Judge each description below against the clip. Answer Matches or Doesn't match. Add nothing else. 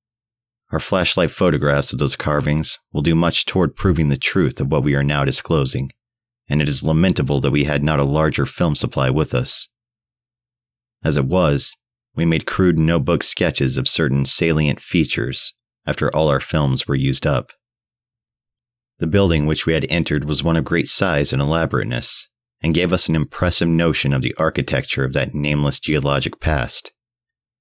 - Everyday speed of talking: Matches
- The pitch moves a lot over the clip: Matches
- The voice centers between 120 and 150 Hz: Doesn't match